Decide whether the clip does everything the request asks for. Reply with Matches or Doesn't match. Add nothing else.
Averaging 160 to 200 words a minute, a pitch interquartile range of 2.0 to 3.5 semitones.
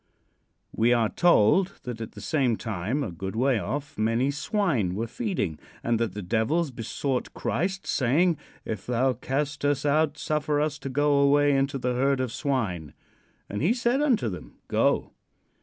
Doesn't match